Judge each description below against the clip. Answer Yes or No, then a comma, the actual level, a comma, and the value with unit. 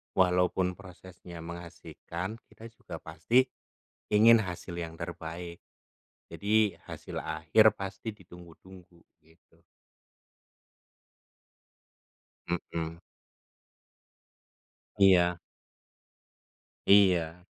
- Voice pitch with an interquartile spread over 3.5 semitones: No, narrow, 2.4 semitones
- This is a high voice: No, very low, 90 Hz